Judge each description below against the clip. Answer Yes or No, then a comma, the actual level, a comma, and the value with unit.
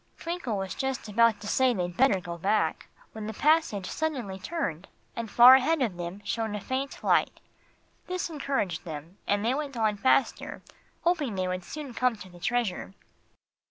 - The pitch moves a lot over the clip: Yes, wide, 5.8 semitones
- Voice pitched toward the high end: Yes, high, 220 Hz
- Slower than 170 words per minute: No, average, 175 wpm